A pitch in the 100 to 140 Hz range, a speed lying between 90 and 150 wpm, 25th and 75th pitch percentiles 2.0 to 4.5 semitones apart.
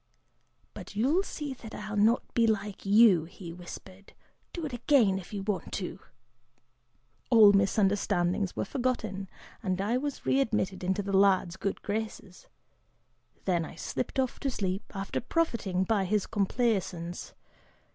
No: high, 205 Hz; average, 140 wpm; average, 3.5 semitones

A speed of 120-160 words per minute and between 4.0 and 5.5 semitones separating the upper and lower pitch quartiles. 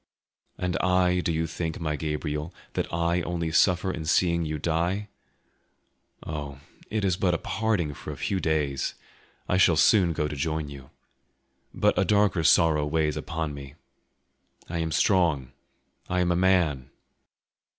No: average, 155 wpm; average, 3.0 semitones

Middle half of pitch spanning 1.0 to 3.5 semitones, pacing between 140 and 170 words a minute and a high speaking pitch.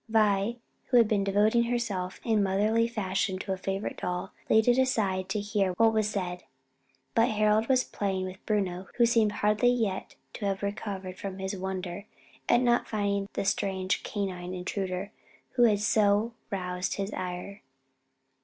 Yes: narrow, 2.5 semitones; average, 165 wpm; high, 200 Hz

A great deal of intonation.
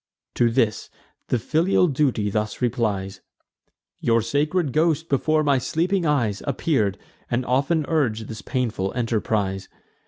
Yes: wide, 5.9 semitones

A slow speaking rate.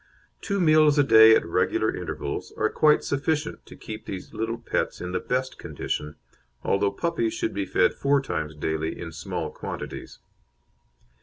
No: average, 160 wpm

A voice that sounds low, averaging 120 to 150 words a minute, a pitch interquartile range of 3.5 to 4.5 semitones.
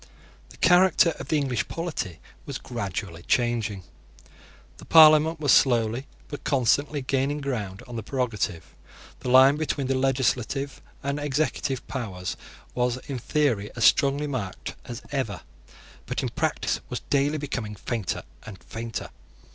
Yes: low, 130 Hz; average, 140 wpm; average, 4.2 semitones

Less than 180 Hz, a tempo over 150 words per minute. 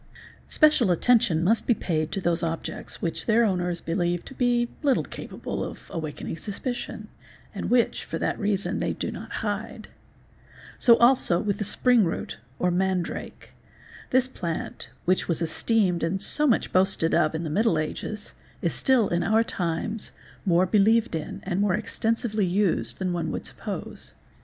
No: high, 190 Hz; average, 165 wpm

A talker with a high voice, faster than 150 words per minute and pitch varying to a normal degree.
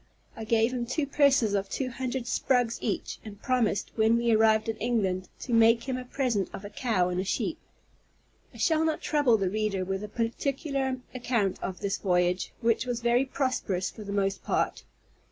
Yes: high, 230 Hz; average, 190 wpm; average, 4.1 semitones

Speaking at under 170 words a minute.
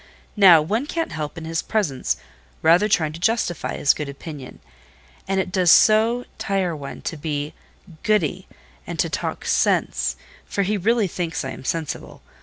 Yes: average, 160 wpm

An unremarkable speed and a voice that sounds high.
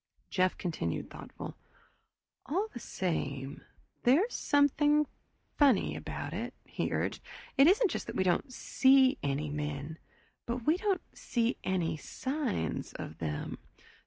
No: slow, 130 wpm; high, 235 Hz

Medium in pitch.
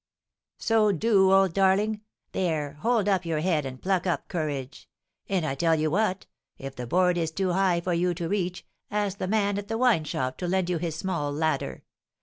Yes: medium, 180 Hz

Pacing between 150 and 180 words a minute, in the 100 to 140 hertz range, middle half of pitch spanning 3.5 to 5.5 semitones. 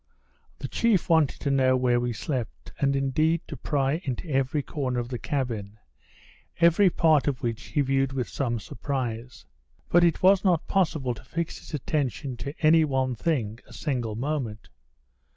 Yes: average, 170 wpm; low, 135 Hz; average, 4.1 semitones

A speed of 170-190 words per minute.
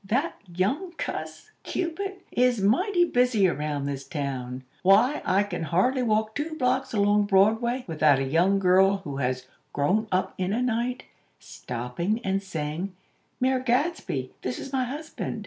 No: average, 150 wpm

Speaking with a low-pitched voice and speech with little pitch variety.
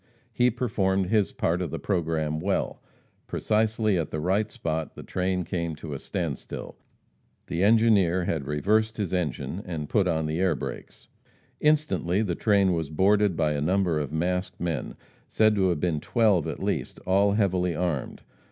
No: very low, 90 Hz; average, 4.2 semitones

